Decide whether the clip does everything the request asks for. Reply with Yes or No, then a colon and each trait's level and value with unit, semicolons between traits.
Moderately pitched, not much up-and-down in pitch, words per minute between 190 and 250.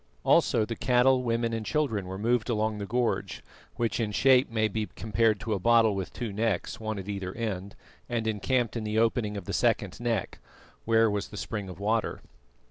No: low, 110 Hz; narrow, 2.2 semitones; average, 200 wpm